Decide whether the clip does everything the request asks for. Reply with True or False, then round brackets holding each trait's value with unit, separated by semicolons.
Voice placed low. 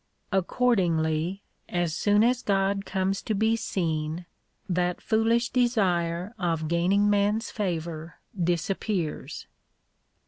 False (190 Hz)